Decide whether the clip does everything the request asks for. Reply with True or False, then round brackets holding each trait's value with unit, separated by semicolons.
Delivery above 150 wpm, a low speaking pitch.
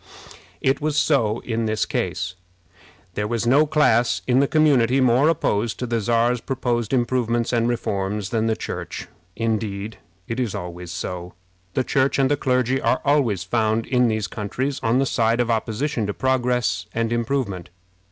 True (165 wpm; 115 Hz)